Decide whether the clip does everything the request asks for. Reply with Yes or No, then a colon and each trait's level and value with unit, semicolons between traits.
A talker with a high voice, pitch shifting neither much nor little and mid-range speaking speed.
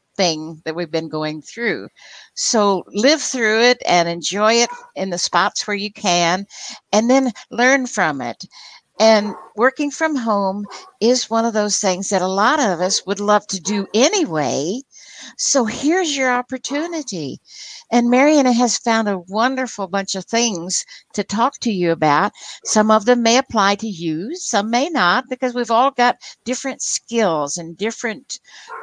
Yes: high, 220 Hz; average, 4.6 semitones; average, 165 wpm